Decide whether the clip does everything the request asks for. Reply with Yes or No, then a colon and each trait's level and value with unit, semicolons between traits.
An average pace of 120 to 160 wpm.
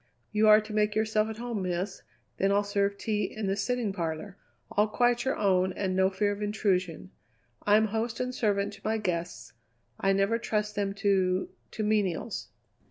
No: average, 180 wpm